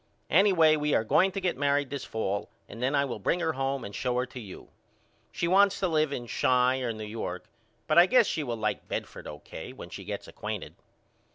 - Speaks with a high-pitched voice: No, low, 135 Hz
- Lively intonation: Yes, wide, 5.8 semitones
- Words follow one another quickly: Yes, fast, 220 wpm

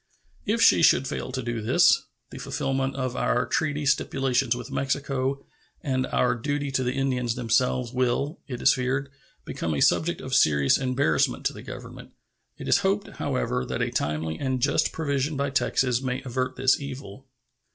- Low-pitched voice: Yes, low, 130 Hz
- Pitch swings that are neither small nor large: No, narrow, 2.0 semitones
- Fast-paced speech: No, average, 170 wpm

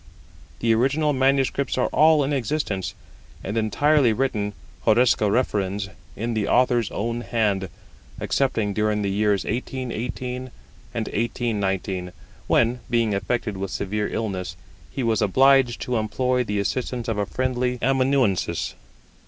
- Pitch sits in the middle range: No, low, 115 Hz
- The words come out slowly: Yes, slow, 130 wpm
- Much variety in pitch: No, average, 3.8 semitones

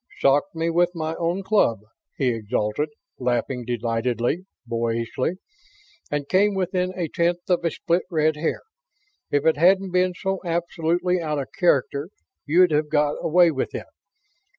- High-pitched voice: No, medium, 160 Hz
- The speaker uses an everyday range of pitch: Yes, average, 4.7 semitones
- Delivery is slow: No, average, 145 wpm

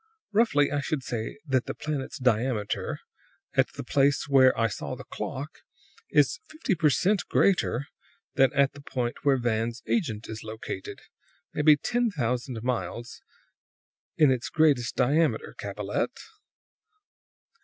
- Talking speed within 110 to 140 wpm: Yes, slow, 135 wpm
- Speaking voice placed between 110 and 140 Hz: Yes, low, 135 Hz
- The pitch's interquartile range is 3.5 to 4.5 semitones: Yes, average, 4.0 semitones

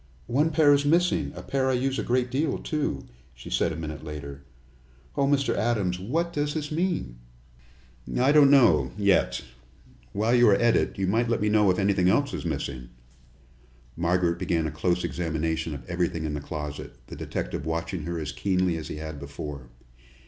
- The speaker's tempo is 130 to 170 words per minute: No, average, 185 wpm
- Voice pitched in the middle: No, very low, 95 Hz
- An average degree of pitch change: No, wide, 8.9 semitones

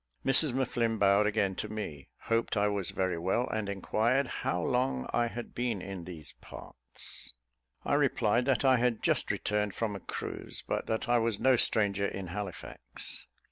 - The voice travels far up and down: No, average, 3.7 semitones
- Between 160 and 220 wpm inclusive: Yes, average, 175 wpm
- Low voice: Yes, low, 105 Hz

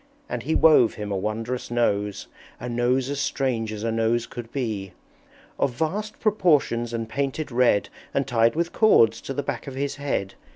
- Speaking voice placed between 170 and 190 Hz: No, low, 120 Hz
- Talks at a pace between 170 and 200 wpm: Yes, average, 180 wpm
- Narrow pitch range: No, average, 3.8 semitones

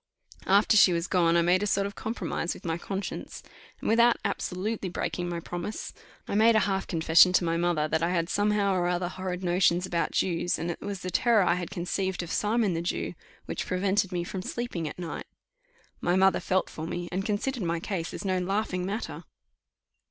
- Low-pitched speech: No, medium, 185 Hz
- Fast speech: Yes, fast, 210 wpm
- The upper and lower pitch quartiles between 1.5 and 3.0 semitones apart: Yes, narrow, 2.6 semitones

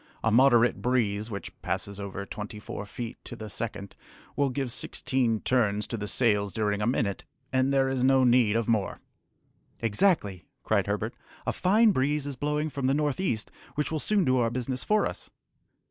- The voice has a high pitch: No, low, 120 Hz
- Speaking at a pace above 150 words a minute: Yes, average, 185 wpm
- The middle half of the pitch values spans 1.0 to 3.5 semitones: No, average, 4.4 semitones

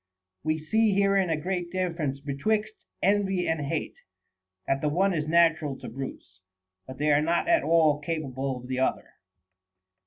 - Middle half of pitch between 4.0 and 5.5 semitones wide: Yes, average, 4.9 semitones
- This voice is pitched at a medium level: Yes, medium, 160 Hz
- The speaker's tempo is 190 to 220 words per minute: No, average, 165 wpm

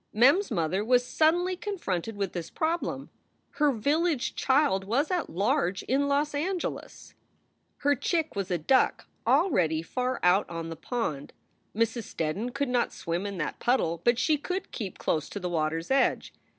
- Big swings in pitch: Yes, wide, 8.4 semitones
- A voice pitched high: Yes, high, 240 Hz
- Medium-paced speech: Yes, average, 170 wpm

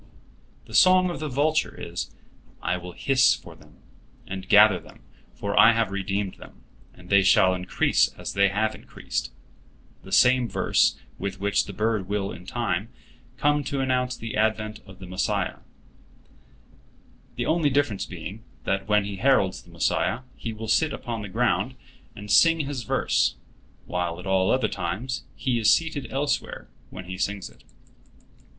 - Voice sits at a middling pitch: No, low, 105 Hz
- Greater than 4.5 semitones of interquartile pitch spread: Yes, average, 5.1 semitones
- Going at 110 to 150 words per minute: No, average, 160 wpm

